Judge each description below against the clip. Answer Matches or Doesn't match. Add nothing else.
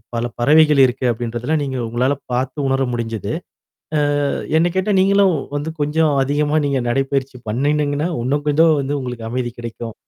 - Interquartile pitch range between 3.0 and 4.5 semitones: Matches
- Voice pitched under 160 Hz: Matches